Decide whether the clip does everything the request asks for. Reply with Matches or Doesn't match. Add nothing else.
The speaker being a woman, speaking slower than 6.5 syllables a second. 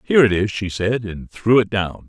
Doesn't match